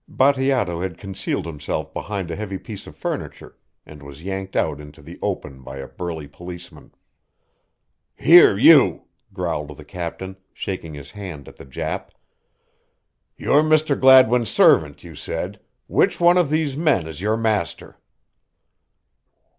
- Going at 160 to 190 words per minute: No, average, 140 wpm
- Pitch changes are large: Yes, wide, 8.3 semitones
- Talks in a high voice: No, very low, 95 Hz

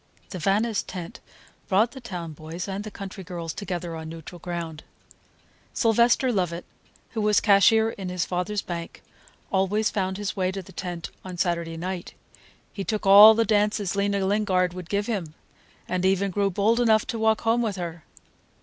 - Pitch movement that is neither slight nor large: Yes, average, 3.1 semitones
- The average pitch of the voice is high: Yes, high, 195 Hz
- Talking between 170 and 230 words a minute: Yes, average, 175 wpm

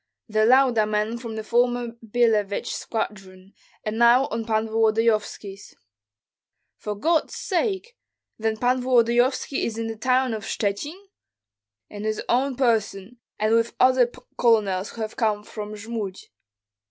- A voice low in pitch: No, high, 225 Hz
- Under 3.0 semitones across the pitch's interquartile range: Yes, narrow, 2.5 semitones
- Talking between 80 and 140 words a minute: Yes, slow, 135 wpm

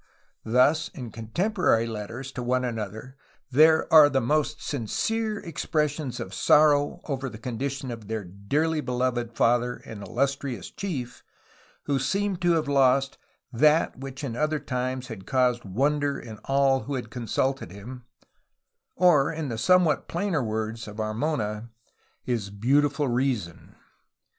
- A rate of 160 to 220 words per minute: No, average, 140 wpm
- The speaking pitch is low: Yes, low, 130 Hz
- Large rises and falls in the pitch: No, average, 4.4 semitones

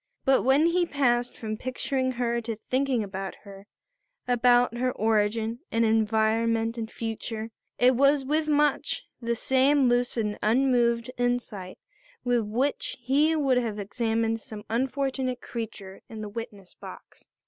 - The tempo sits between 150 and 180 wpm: No, average, 140 wpm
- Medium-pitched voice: No, high, 235 Hz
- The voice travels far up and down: No, average, 2.8 semitones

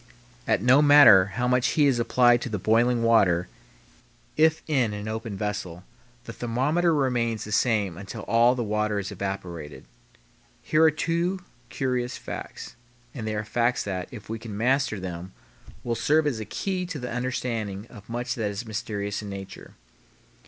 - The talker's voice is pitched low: Yes, low, 115 Hz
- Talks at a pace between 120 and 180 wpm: Yes, average, 170 wpm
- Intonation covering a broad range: No, average, 3.6 semitones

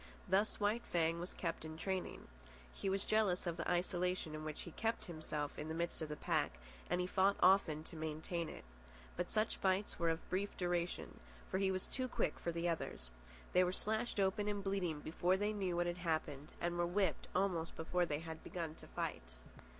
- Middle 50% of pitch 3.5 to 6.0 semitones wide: No, average, 3.0 semitones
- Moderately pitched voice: Yes, medium, 175 Hz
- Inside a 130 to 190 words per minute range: No, average, 200 wpm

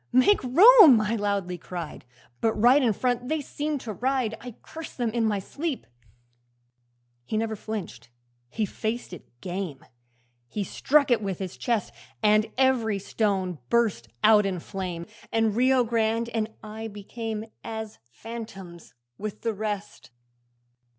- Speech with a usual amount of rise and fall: Yes, average, 3.3 semitones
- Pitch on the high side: Yes, high, 220 Hz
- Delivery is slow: No, average, 145 wpm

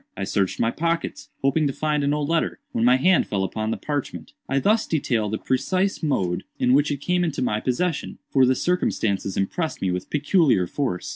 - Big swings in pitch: Yes, wide, 6.7 semitones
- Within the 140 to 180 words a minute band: No, fast, 205 wpm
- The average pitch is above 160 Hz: No, low, 135 Hz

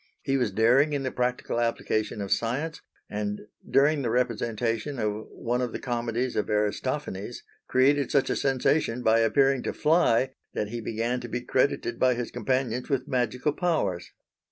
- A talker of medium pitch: No, low, 125 Hz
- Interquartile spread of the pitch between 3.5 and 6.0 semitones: No, average, 3.0 semitones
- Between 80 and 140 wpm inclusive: No, average, 165 wpm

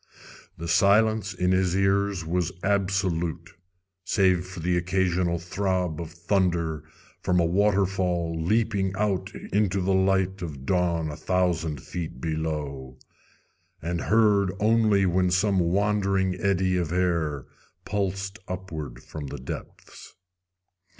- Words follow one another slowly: Yes, slow, 120 wpm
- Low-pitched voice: Yes, very low, 90 Hz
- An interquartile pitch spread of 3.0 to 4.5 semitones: No, narrow, 2.6 semitones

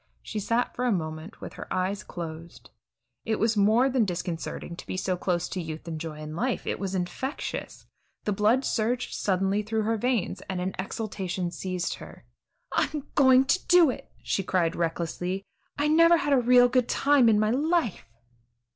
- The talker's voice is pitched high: Yes, high, 205 Hz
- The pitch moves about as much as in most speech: No, wide, 5.7 semitones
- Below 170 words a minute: No, average, 180 wpm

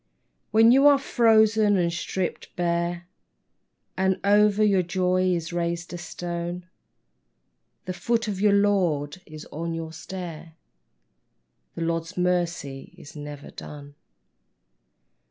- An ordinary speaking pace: No, slow, 120 wpm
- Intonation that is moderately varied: Yes, average, 3.2 semitones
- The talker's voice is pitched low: No, medium, 175 Hz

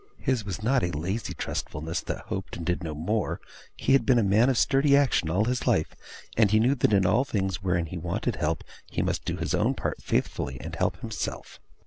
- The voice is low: Yes, low, 100 Hz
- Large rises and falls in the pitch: Yes, wide, 5.8 semitones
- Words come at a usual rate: No, fast, 220 wpm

